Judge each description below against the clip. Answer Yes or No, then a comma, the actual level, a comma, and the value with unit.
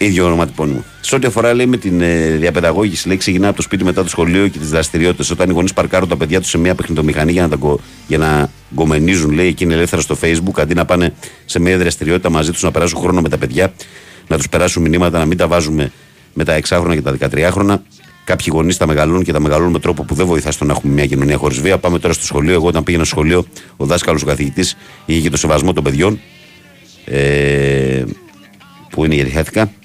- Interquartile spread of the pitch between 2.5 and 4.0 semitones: Yes, average, 2.9 semitones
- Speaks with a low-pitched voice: Yes, very low, 85 Hz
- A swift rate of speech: Yes, fast, 220 wpm